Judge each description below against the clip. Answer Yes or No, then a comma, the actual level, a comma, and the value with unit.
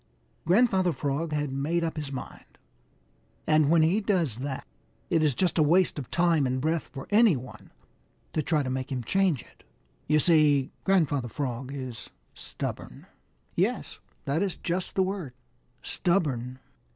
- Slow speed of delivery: No, average, 155 wpm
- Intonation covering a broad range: No, average, 4.5 semitones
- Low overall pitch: No, medium, 155 Hz